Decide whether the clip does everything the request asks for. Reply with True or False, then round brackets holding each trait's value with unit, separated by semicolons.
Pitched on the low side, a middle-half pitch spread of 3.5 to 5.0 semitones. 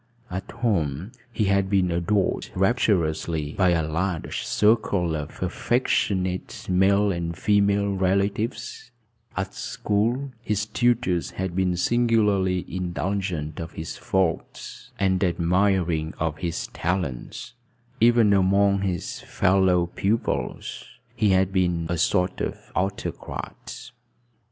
False (95 Hz; 2.8 semitones)